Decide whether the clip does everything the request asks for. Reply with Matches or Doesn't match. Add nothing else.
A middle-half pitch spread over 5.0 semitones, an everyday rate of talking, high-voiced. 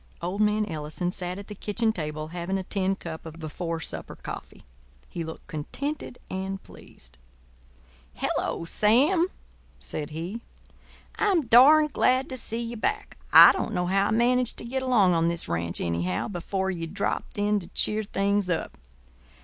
Matches